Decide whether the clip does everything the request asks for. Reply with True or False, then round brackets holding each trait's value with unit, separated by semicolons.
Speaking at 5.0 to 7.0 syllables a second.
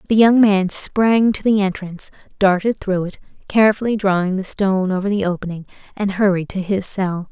True (5.4 syllables/s)